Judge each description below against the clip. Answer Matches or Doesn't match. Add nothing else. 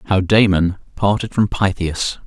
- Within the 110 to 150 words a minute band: Matches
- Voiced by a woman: Doesn't match